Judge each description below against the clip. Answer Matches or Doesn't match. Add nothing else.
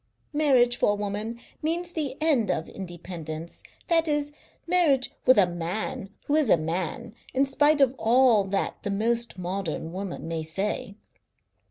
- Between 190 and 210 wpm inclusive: Doesn't match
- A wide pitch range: Matches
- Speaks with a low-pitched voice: Doesn't match